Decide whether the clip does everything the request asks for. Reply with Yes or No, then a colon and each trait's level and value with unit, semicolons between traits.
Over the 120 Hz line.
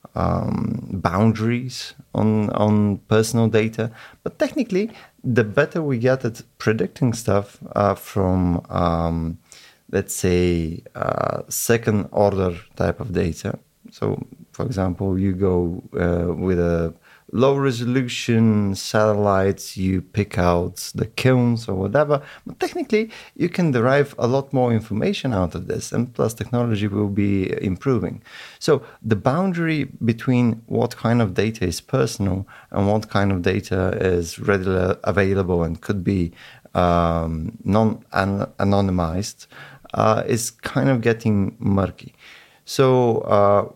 No: low, 105 Hz